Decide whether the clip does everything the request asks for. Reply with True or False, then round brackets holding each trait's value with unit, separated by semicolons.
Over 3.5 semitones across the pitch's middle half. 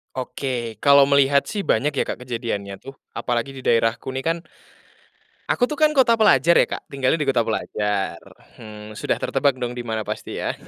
True (3.9 semitones)